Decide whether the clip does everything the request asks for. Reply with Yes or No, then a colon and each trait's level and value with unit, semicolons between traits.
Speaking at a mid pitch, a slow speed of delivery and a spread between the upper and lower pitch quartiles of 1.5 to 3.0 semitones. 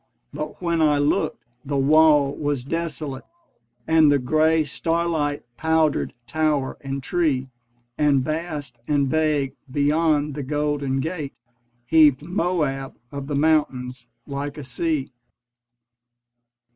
Yes: medium, 145 Hz; slow, 115 wpm; narrow, 2.4 semitones